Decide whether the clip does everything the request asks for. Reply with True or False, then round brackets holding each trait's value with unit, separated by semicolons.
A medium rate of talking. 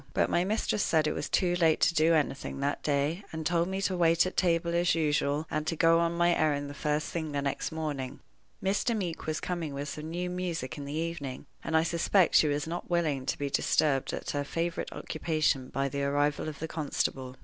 False (225 wpm)